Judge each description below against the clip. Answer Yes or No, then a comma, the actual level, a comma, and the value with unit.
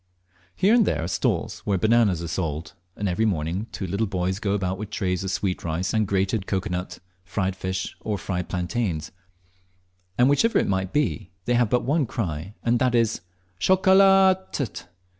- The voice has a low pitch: Yes, low, 100 Hz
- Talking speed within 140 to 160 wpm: No, average, 185 wpm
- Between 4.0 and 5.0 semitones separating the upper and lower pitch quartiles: Yes, average, 4.7 semitones